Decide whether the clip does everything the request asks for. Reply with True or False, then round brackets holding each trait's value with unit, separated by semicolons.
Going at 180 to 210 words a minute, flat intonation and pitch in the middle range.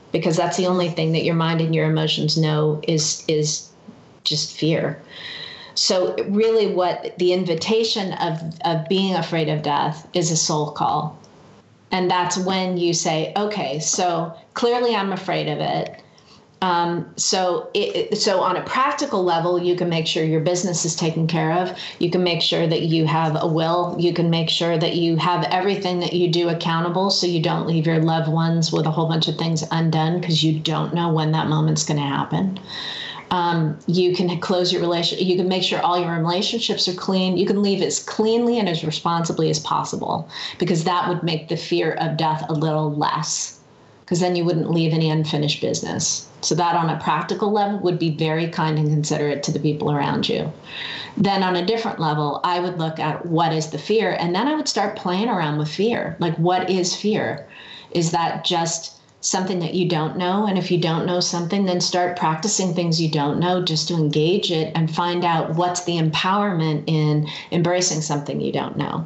True (200 wpm; 2.3 semitones; 170 Hz)